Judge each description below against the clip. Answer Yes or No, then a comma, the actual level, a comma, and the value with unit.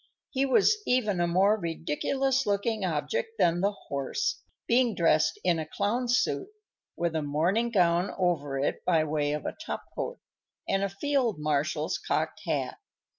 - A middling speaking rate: Yes, average, 160 wpm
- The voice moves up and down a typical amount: No, wide, 6.9 semitones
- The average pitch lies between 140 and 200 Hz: Yes, high, 190 Hz